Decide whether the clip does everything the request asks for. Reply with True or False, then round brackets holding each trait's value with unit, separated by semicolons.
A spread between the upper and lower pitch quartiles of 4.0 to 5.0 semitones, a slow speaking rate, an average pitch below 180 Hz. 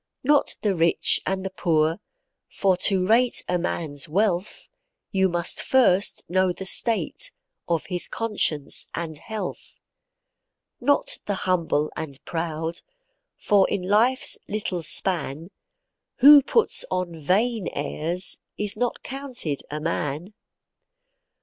False (4.6 semitones; 120 wpm; 185 Hz)